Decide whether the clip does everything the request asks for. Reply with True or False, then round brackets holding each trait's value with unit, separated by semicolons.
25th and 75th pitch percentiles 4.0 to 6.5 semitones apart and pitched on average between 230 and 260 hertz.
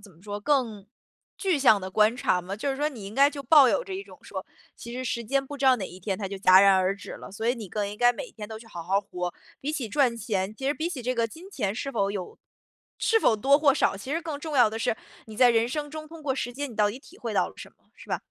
True (5.5 semitones; 235 Hz)